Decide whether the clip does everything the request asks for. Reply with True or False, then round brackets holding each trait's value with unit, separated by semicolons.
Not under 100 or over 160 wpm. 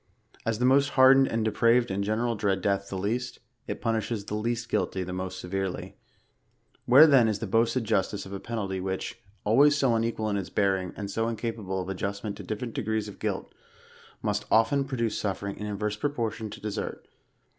False (190 wpm)